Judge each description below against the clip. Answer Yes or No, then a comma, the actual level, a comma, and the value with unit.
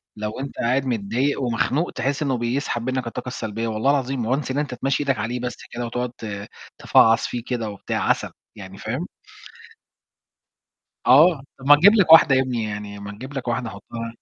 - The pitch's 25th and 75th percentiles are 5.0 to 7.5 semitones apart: No, average, 3.0 semitones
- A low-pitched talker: Yes, low, 125 Hz